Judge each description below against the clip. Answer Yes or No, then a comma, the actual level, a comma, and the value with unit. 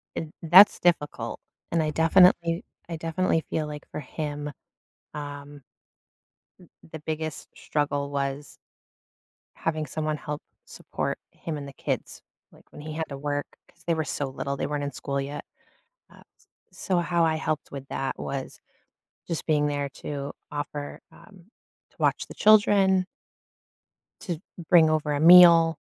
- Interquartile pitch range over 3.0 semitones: No, narrow, 2.5 semitones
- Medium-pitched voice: Yes, medium, 155 Hz